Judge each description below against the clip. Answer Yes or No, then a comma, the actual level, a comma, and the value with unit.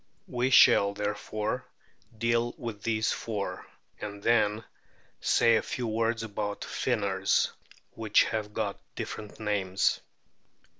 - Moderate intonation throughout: No, narrow, 2.1 semitones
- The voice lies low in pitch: Yes, low, 110 Hz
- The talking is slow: Yes, slow, 120 wpm